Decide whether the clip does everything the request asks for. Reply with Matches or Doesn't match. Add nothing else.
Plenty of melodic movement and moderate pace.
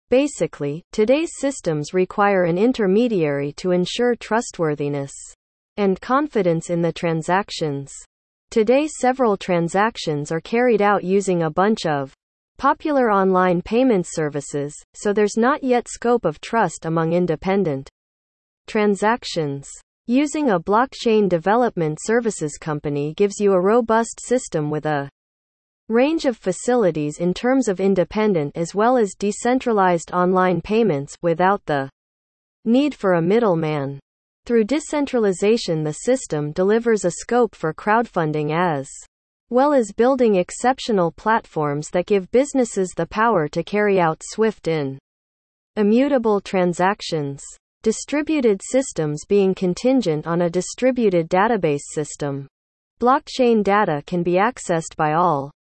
Doesn't match